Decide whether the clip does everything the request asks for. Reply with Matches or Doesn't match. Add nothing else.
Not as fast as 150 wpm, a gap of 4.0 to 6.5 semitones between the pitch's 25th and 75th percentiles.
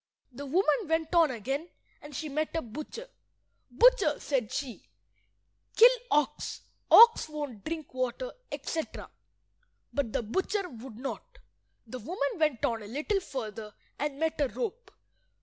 Matches